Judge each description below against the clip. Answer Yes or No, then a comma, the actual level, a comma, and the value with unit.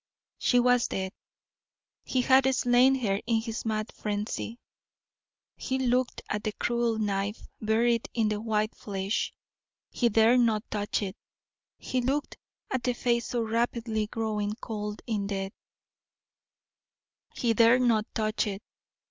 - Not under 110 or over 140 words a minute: Yes, slow, 135 wpm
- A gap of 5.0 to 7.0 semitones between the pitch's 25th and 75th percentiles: No, narrow, 2.4 semitones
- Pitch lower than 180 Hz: No, high, 225 Hz